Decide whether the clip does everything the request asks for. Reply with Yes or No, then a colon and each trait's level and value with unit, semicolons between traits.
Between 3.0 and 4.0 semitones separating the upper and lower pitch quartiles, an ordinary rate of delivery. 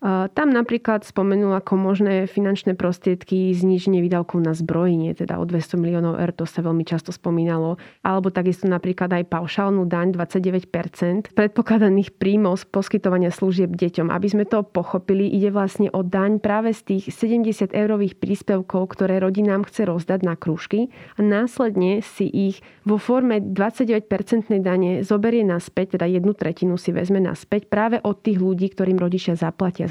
No: narrow, 2.5 semitones; average, 155 wpm